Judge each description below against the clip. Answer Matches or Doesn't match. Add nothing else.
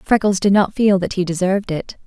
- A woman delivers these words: Matches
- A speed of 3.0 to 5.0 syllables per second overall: Doesn't match